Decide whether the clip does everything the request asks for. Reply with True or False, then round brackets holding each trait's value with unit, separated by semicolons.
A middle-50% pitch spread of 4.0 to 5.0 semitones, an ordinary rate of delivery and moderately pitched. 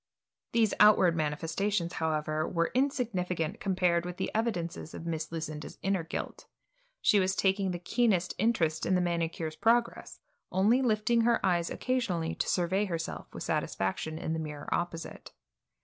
True (4.3 semitones; 150 wpm; 180 Hz)